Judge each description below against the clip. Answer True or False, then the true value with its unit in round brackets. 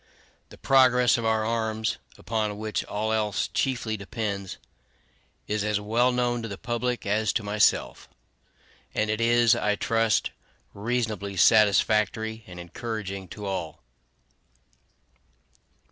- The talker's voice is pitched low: True (110 Hz)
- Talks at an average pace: False (120 wpm)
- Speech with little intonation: True (2.0 semitones)